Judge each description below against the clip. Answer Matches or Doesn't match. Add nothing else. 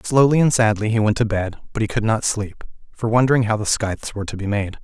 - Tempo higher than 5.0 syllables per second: Matches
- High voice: Doesn't match